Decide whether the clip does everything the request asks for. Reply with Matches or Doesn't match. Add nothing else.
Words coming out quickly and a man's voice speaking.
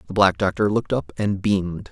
Matches